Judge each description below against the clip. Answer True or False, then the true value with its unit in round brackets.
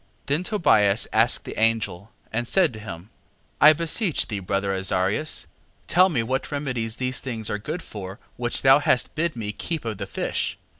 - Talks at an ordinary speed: True (185 wpm)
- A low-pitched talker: True (115 Hz)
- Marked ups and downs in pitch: True (6.4 semitones)